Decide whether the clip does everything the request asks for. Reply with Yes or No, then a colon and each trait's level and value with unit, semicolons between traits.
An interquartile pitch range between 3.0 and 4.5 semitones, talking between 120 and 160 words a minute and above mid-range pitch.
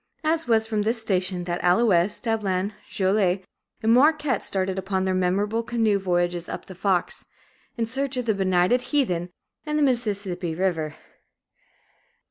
Yes: average, 4.1 semitones; average, 140 wpm; high, 200 Hz